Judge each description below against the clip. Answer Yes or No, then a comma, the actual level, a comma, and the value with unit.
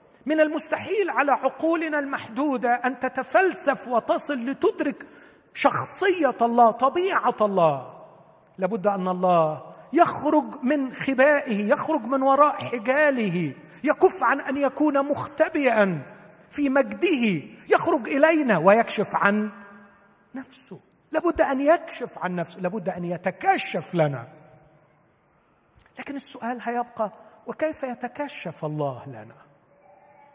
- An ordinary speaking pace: Yes, average, 100 wpm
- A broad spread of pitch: Yes, wide, 7.4 semitones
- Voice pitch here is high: Yes, high, 245 Hz